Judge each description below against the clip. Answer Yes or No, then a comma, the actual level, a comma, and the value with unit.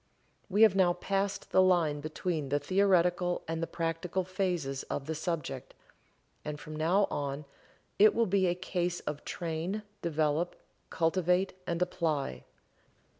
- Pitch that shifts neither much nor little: Yes, average, 3.2 semitones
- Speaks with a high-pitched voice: No, medium, 175 Hz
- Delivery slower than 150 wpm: Yes, average, 140 wpm